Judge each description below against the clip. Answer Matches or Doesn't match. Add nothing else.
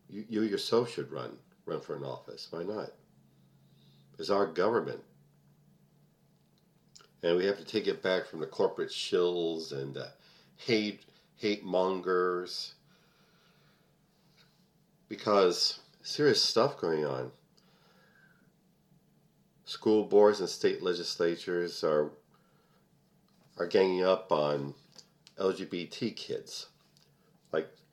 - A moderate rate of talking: Doesn't match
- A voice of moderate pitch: Doesn't match